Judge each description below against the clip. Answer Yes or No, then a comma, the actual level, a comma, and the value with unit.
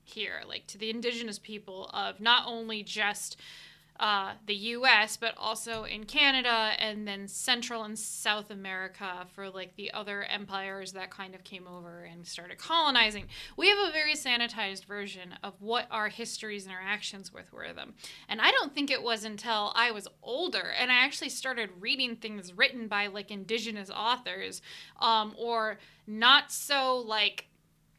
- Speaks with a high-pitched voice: Yes, high, 215 Hz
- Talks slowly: No, average, 165 wpm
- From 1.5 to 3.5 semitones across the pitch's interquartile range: Yes, average, 2.7 semitones